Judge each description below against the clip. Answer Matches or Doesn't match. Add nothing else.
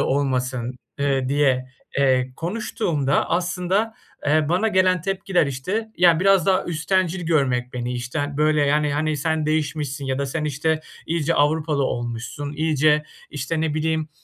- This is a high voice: Doesn't match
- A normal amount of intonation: Matches